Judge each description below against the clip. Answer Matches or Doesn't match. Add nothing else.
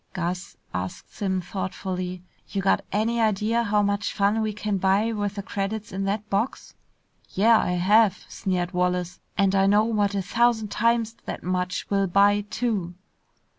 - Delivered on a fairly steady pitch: Matches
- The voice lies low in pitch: Doesn't match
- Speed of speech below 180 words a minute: Matches